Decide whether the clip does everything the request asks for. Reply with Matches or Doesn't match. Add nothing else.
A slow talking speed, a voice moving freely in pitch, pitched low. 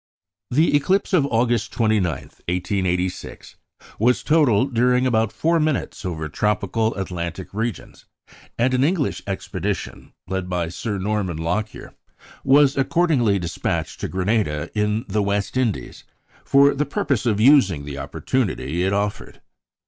Matches